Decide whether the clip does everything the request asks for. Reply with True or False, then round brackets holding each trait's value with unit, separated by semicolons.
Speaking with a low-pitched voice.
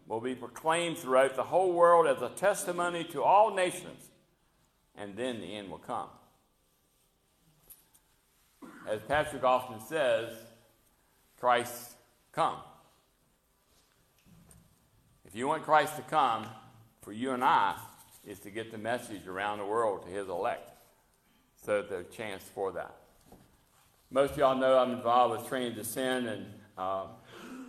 True (125 Hz)